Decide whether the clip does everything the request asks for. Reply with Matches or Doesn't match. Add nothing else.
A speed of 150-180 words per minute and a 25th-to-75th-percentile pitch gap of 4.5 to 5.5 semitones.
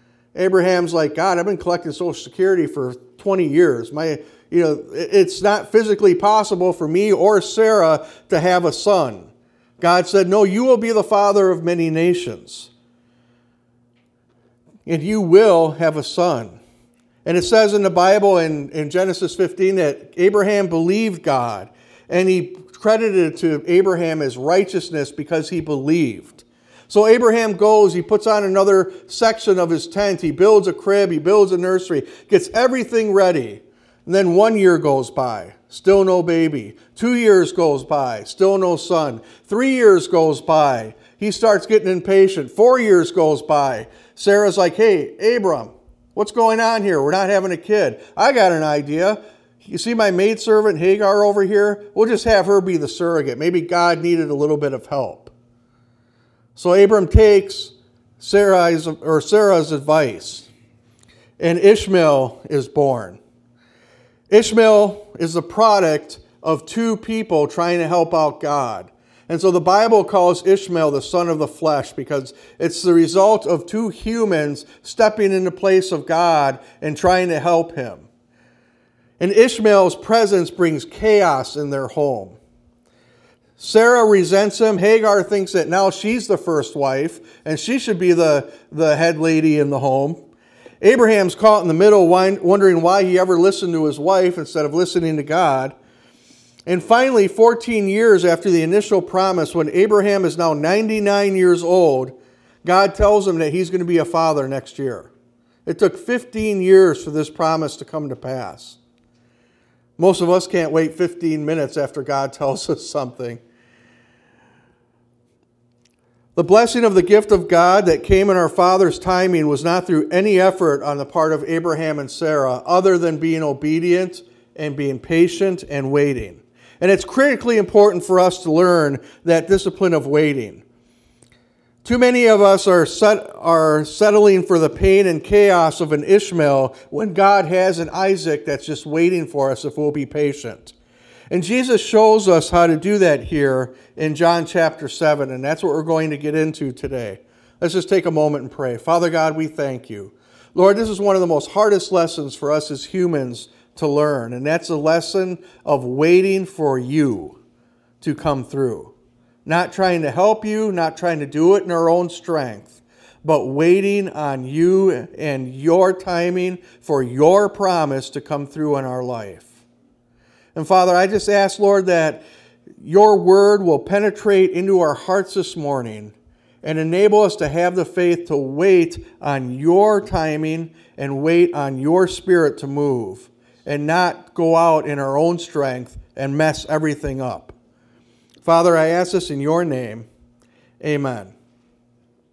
Matches